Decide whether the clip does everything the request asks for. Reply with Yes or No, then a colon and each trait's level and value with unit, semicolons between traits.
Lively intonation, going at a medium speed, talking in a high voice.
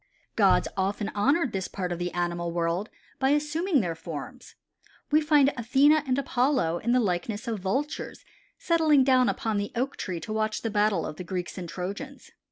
Yes: wide, 7.4 semitones; average, 180 wpm; high, 215 Hz